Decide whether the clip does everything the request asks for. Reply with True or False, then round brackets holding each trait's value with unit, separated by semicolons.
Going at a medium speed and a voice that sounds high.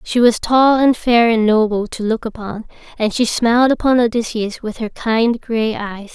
True (195 wpm; 225 Hz)